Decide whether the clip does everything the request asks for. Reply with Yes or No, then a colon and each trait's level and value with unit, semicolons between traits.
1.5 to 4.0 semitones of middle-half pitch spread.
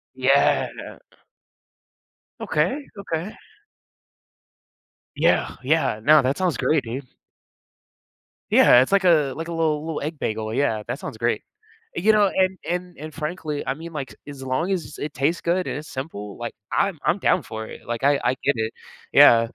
No: average, 4.6 semitones